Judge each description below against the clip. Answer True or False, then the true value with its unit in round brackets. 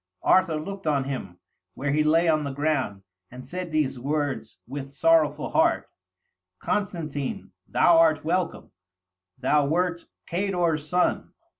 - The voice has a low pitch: False (155 Hz)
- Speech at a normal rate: False (130 wpm)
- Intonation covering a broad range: False (3.5 semitones)